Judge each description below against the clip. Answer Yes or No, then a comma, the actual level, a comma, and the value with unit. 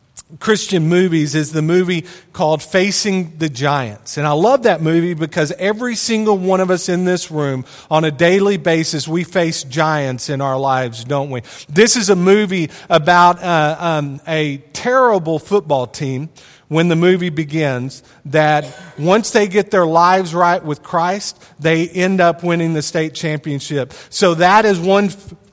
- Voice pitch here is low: No, medium, 165 Hz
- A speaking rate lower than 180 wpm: Yes, average, 165 wpm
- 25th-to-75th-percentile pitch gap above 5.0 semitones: No, average, 3.6 semitones